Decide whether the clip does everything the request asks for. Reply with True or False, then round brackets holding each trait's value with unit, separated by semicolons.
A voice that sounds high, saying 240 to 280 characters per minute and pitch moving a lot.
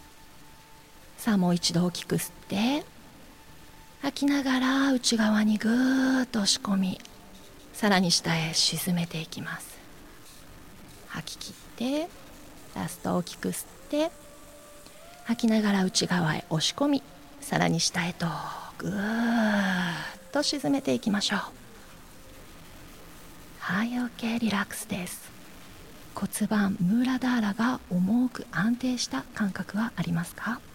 False (215 Hz; 230 characters per minute; 5.7 semitones)